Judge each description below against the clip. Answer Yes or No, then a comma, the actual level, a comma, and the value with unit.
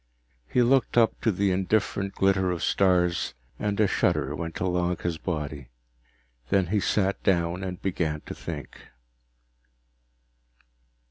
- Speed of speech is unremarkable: No, slow, 130 wpm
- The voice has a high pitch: No, very low, 90 Hz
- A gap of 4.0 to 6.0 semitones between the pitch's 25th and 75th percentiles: No, narrow, 2.6 semitones